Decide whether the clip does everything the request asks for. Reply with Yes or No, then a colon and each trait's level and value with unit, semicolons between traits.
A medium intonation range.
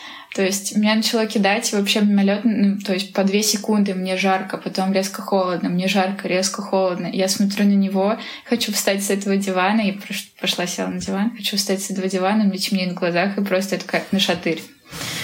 No: narrow, 1.7 semitones